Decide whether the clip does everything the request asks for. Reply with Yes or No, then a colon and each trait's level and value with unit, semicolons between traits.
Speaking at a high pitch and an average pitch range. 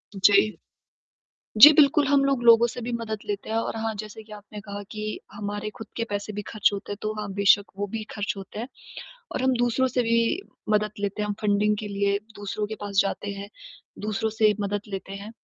No: high, 210 Hz; narrow, 1.9 semitones